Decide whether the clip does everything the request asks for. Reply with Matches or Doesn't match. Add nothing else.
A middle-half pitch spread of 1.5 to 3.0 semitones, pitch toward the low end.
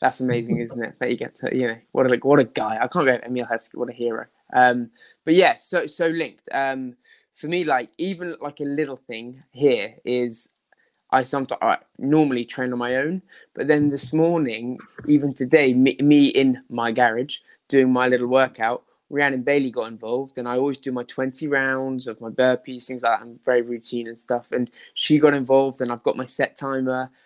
Matches